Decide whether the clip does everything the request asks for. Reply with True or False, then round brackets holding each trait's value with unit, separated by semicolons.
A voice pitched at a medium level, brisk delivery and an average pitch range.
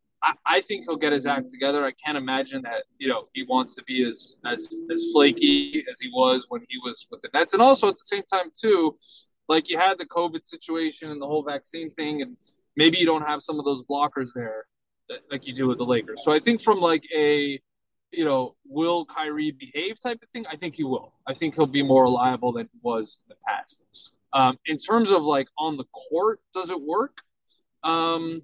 False (155 Hz; 225 wpm; 6.2 semitones)